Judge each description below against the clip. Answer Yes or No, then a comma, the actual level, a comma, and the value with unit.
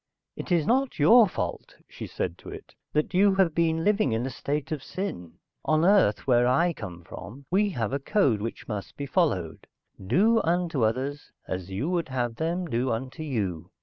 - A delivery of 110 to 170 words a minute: No, average, 190 wpm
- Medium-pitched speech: Yes, medium, 145 Hz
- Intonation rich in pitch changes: Yes, wide, 7.5 semitones